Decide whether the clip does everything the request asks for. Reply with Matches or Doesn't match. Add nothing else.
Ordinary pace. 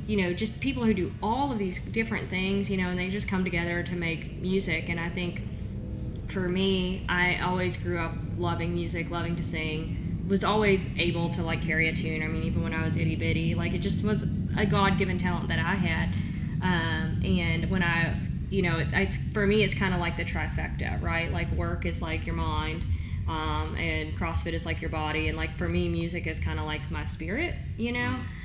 Doesn't match